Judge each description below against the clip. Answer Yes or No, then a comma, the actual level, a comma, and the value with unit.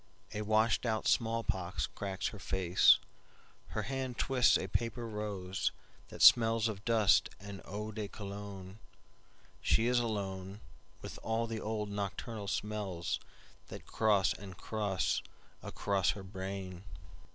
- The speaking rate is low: Yes, slow, 105 wpm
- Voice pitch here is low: Yes, low, 105 Hz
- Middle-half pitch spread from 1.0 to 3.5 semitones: Yes, narrow, 2.6 semitones